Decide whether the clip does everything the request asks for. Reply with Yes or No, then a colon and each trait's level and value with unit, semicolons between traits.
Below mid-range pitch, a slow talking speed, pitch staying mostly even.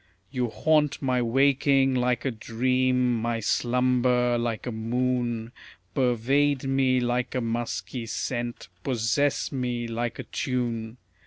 Yes: low, 125 Hz; slow, 120 wpm; narrow, 1.6 semitones